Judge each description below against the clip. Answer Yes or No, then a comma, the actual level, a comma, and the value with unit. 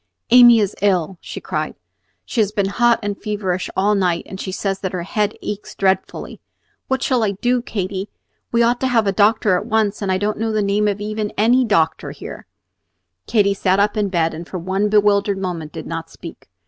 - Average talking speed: No, fast, 210 wpm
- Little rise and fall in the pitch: Yes, narrow, 2.2 semitones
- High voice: Yes, high, 205 Hz